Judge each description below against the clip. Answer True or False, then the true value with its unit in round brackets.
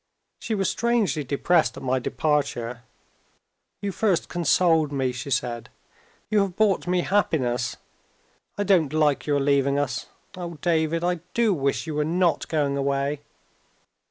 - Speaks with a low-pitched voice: False (155 Hz)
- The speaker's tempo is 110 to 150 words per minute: True (145 wpm)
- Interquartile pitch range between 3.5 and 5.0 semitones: True (4.4 semitones)